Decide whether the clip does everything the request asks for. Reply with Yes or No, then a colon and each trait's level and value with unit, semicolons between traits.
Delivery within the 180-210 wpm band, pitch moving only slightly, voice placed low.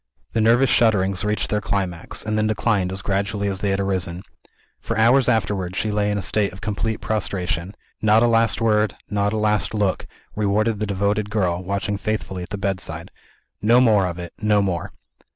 Yes: average, 190 wpm; narrow, 2.1 semitones; low, 105 Hz